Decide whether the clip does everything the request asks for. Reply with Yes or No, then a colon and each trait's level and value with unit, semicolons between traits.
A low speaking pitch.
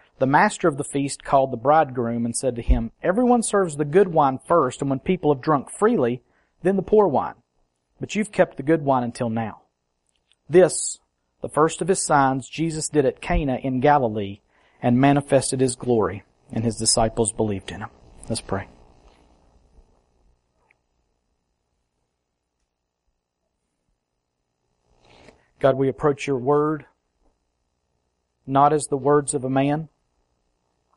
Yes: low, 115 Hz